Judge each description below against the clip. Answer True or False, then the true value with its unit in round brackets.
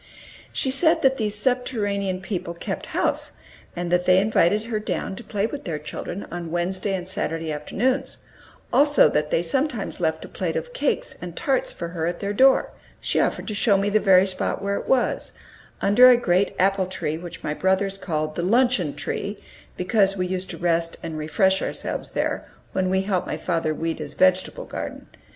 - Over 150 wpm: True (190 wpm)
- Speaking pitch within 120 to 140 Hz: False (190 Hz)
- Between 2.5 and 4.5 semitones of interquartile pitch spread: True (3.7 semitones)